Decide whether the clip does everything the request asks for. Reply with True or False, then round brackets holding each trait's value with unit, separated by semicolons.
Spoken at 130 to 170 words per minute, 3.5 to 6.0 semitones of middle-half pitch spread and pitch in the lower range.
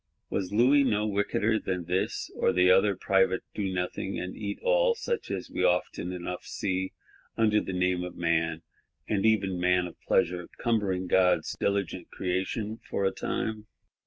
False (155 wpm; 2.7 semitones; 95 Hz)